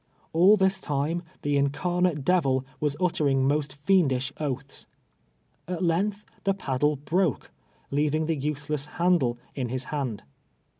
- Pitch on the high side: No, medium, 150 Hz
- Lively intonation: No, average, 4.4 semitones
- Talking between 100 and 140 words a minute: Yes, slow, 135 wpm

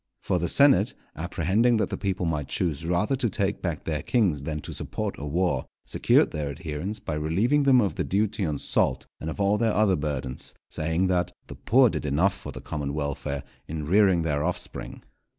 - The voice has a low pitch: Yes, very low, 85 Hz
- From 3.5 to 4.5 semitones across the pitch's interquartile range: No, average, 5.1 semitones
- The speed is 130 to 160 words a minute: No, average, 200 wpm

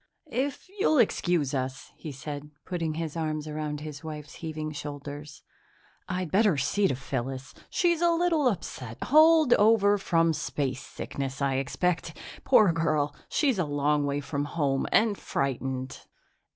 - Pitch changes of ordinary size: No, wide, 5.8 semitones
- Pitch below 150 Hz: No, medium, 155 Hz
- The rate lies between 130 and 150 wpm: Yes, average, 140 wpm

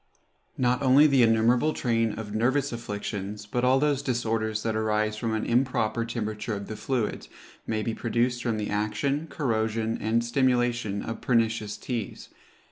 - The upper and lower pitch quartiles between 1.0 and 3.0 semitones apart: Yes, narrow, 2.5 semitones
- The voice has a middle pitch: No, low, 115 Hz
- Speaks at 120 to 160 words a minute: Yes, average, 155 wpm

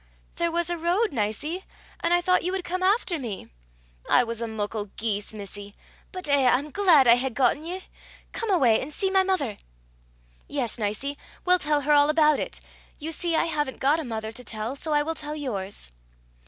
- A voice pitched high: Yes, very high, 295 Hz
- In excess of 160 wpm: Yes, average, 200 wpm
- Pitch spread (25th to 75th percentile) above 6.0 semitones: Yes, wide, 6.7 semitones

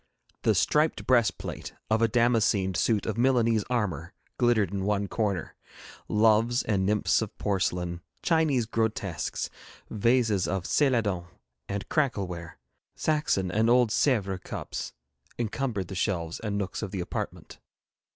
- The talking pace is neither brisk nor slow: No, slow, 130 wpm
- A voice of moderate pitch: No, low, 105 Hz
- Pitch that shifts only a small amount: No, average, 3.8 semitones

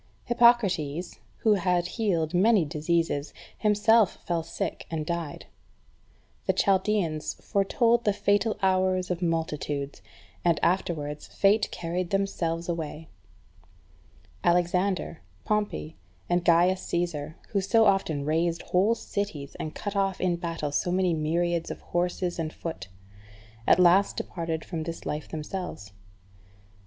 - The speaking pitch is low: No, medium, 175 Hz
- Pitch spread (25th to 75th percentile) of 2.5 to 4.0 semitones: Yes, average, 3.3 semitones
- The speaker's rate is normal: No, slow, 125 wpm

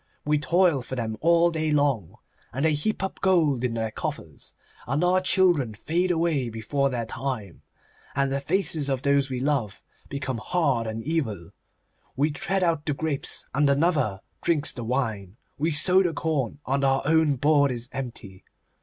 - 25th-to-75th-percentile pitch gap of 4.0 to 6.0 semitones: Yes, average, 4.5 semitones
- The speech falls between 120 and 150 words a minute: No, average, 170 wpm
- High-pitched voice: No, medium, 140 Hz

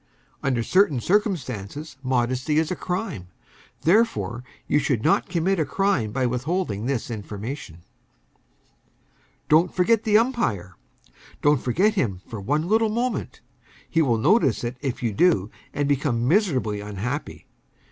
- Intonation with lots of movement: Yes, wide, 7.7 semitones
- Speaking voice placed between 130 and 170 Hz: Yes, medium, 140 Hz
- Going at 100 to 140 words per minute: Yes, slow, 135 wpm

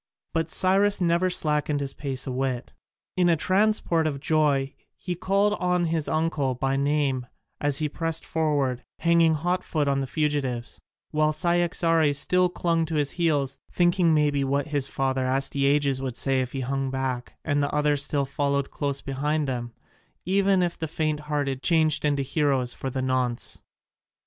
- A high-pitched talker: No, medium, 145 Hz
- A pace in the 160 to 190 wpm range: Yes, average, 165 wpm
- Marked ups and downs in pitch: No, average, 3.4 semitones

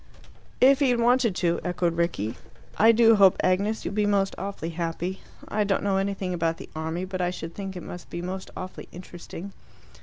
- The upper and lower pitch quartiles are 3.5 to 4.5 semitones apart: No, average, 2.9 semitones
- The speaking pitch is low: No, medium, 185 Hz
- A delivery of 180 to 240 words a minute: Yes, average, 200 wpm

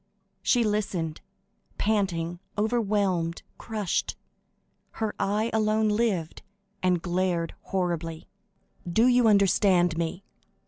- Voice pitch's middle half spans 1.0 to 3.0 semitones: No, average, 3.8 semitones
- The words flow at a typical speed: No, slow, 90 wpm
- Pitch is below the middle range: No, high, 195 Hz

